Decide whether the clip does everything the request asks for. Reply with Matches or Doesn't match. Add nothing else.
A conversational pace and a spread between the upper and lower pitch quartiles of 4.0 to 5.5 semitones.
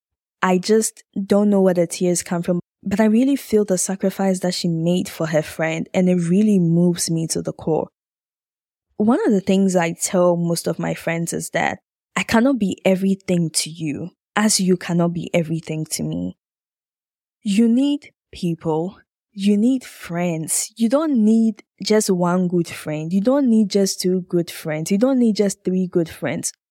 Doesn't match